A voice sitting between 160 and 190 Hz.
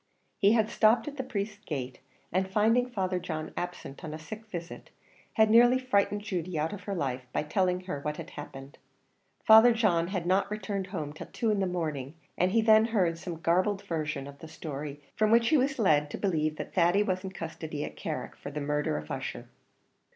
Yes: medium, 185 Hz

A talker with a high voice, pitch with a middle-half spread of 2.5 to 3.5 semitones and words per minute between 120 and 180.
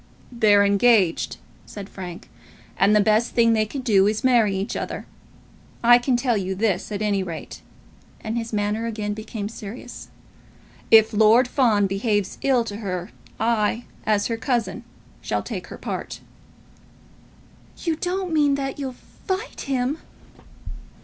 Yes: high, 220 Hz; average, 3.1 semitones; average, 150 wpm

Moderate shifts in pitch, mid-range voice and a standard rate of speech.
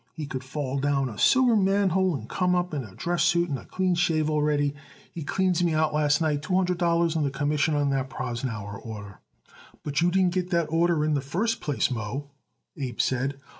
No: average, 4.3 semitones; medium, 150 Hz; fast, 210 wpm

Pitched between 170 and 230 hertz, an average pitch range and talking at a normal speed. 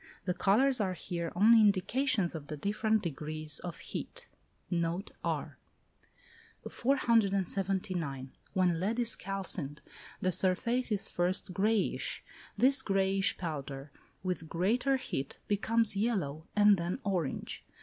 No: high, 190 Hz; average, 4.3 semitones; slow, 120 wpm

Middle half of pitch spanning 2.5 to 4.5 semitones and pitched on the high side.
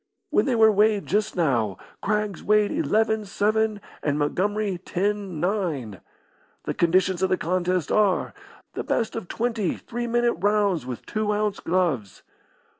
Yes: average, 3.5 semitones; high, 200 Hz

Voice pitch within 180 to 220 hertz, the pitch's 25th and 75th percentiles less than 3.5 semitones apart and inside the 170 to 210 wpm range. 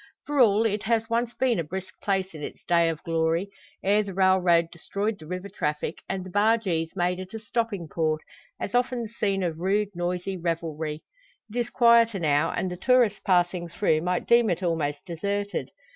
No: medium, 185 Hz; average, 4.0 semitones; average, 190 wpm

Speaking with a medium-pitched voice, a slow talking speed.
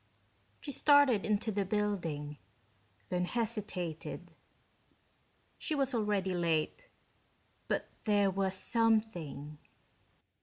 No: high, 205 Hz; slow, 85 wpm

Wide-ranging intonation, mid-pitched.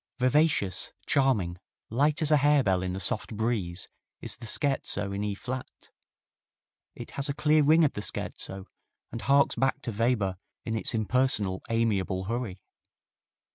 No: wide, 5.8 semitones; low, 115 Hz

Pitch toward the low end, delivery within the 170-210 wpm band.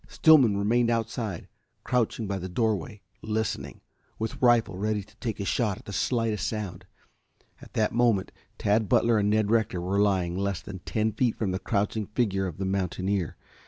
Yes: low, 105 Hz; average, 175 wpm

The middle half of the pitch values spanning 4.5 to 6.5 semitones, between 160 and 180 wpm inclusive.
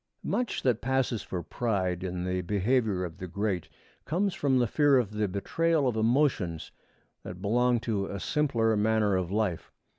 Yes: average, 5.3 semitones; average, 170 wpm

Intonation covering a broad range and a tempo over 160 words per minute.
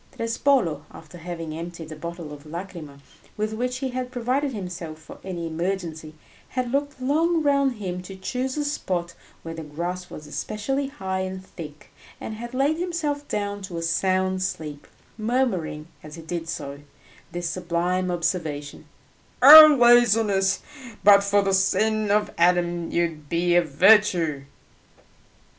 No: wide, 6.2 semitones; average, 150 wpm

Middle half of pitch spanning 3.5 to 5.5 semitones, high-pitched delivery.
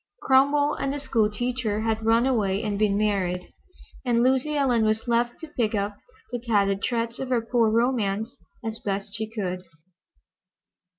No: average, 3.1 semitones; high, 225 Hz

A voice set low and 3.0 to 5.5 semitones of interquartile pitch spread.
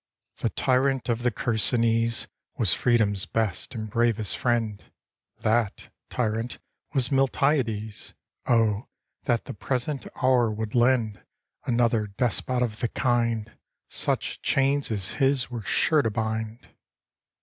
No: low, 115 Hz; narrow, 2.4 semitones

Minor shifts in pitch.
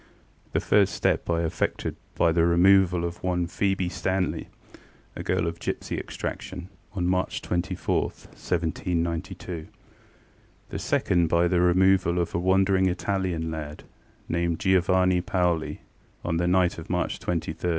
Yes: narrow, 1.6 semitones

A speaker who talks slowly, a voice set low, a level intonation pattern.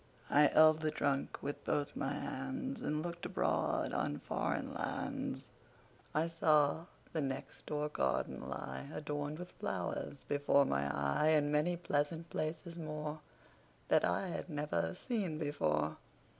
No: slow, 120 wpm; medium, 150 Hz; narrow, 2.1 semitones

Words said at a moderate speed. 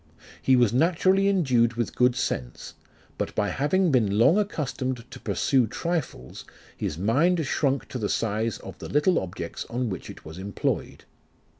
Yes: average, 160 wpm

